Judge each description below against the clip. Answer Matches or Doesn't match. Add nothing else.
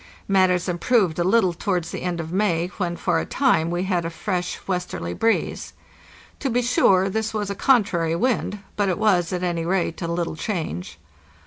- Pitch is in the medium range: Matches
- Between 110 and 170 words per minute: Doesn't match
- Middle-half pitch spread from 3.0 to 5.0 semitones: Matches